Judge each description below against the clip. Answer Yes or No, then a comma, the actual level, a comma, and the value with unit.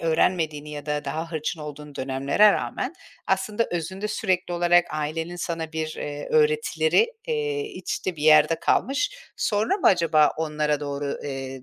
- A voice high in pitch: No, medium, 165 Hz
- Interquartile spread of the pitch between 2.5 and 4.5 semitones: No, wide, 5.6 semitones